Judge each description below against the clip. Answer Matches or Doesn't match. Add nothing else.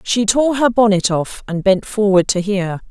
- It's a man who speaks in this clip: Doesn't match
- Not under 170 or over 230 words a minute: Matches